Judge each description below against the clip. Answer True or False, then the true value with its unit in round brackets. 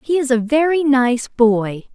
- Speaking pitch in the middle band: False (260 Hz)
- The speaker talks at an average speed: True (185 wpm)